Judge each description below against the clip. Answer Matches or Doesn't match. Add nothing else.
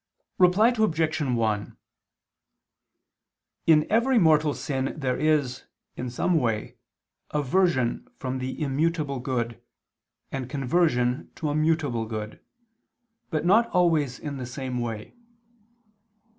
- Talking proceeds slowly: Matches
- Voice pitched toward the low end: Doesn't match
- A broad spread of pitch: Doesn't match